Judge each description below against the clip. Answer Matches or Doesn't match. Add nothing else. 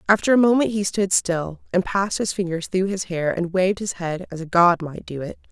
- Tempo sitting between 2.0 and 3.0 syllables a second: Doesn't match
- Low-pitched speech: Doesn't match